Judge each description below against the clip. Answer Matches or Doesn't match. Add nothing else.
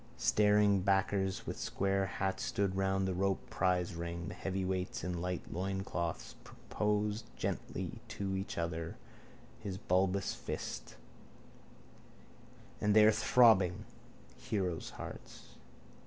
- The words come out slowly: Matches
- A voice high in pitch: Doesn't match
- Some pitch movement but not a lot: Doesn't match